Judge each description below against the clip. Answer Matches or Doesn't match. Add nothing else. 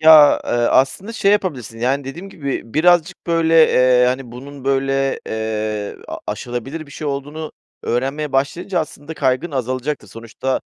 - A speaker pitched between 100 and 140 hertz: Matches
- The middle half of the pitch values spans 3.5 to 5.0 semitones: Matches